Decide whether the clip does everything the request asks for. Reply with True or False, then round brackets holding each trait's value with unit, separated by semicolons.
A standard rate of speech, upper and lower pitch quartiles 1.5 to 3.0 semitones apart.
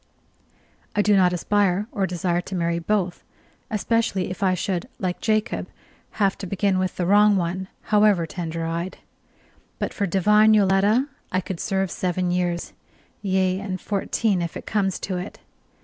True (160 wpm; 2.5 semitones)